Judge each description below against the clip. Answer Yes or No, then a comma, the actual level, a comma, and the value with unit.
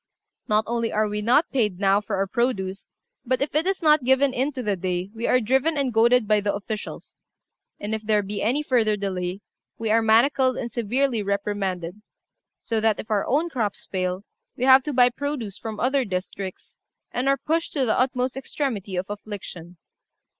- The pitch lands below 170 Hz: No, high, 225 Hz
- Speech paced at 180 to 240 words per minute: Yes, average, 190 wpm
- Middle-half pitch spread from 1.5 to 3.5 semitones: No, average, 4.4 semitones